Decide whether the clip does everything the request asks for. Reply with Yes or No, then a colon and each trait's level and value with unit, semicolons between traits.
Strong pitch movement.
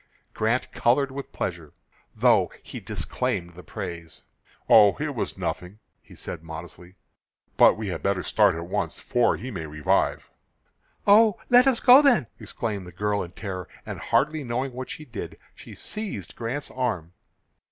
Yes: wide, 6.9 semitones